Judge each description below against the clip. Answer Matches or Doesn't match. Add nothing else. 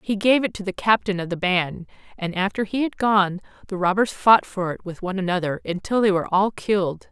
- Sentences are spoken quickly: Matches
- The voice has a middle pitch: Doesn't match